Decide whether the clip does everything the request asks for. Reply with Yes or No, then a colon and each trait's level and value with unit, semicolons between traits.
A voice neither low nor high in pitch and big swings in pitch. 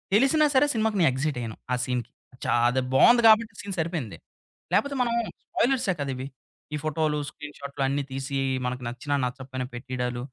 Yes: medium, 145 Hz; wide, 8.4 semitones